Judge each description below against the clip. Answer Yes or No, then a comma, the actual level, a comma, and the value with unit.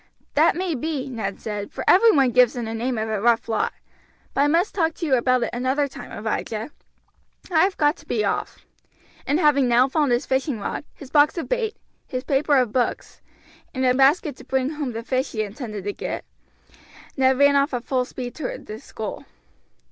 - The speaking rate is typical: No, fast, 210 wpm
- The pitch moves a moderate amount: Yes, average, 3.7 semitones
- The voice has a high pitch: Yes, very high, 260 Hz